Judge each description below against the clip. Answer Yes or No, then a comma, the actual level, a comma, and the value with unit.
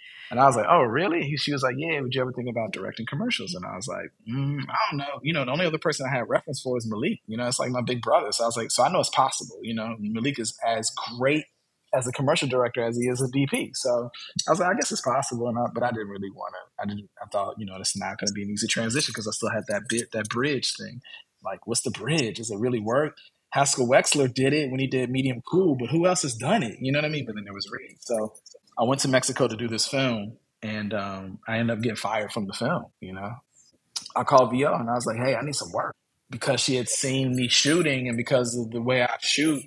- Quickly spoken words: Yes, fast, 280 wpm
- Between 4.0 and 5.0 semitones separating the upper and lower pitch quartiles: No, average, 3.5 semitones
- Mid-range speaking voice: No, low, 125 Hz